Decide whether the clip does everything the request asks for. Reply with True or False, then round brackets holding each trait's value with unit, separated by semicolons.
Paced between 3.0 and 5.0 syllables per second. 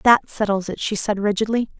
False (5.3 syllables/s)